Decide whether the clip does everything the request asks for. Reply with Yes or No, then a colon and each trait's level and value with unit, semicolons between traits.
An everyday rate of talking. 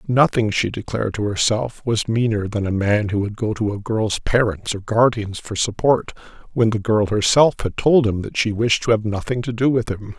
No: fast, 225 wpm